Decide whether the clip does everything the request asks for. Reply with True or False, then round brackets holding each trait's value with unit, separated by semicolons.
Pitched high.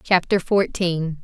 False (175 Hz)